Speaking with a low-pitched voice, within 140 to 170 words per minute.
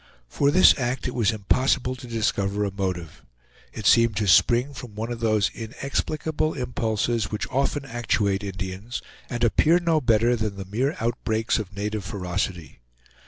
Yes: low, 115 Hz; average, 160 wpm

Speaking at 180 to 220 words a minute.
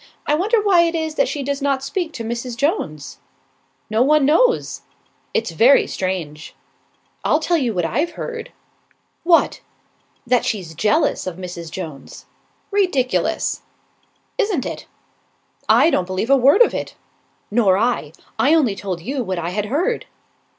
No: average, 150 wpm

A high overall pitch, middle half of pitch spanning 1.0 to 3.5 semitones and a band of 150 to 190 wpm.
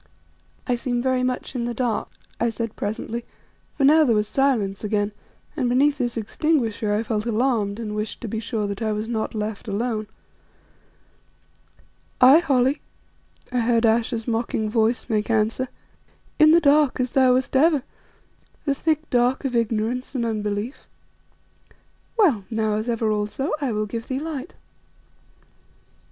Yes: high, 235 Hz; average, 3.2 semitones; average, 155 wpm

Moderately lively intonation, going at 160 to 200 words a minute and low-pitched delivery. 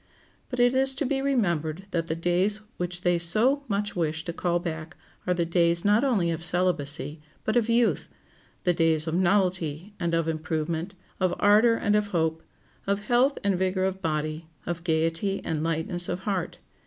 No: average, 3.9 semitones; average, 180 wpm; medium, 175 Hz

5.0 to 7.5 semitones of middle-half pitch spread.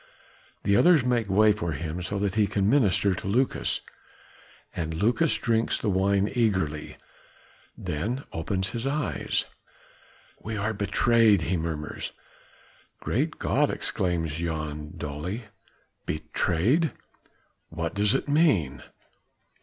Yes: wide, 5.6 semitones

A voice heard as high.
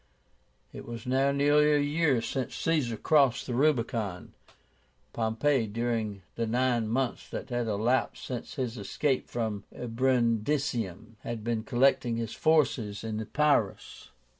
No: low, 120 Hz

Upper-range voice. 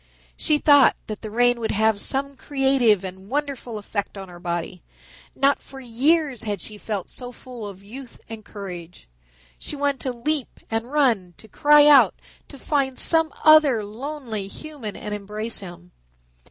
Yes: high, 235 Hz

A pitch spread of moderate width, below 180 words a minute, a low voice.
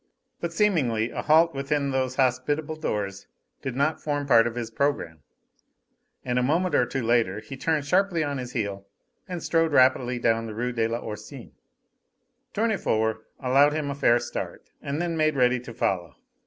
Yes: average, 4.6 semitones; average, 170 wpm; low, 130 Hz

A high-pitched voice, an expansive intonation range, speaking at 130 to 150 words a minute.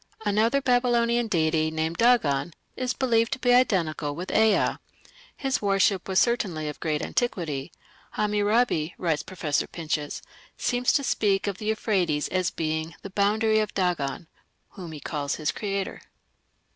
Yes: high, 195 Hz; wide, 6.1 semitones; average, 145 wpm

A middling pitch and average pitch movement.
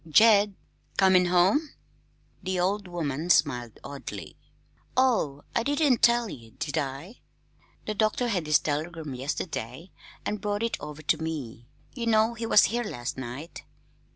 No: medium, 180 Hz; wide, 6.9 semitones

